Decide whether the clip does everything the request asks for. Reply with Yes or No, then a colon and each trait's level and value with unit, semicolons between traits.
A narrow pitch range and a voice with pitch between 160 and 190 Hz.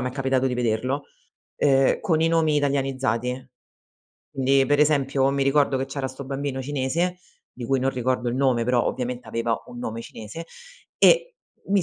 No: narrow, 2.2 semitones; low, 135 Hz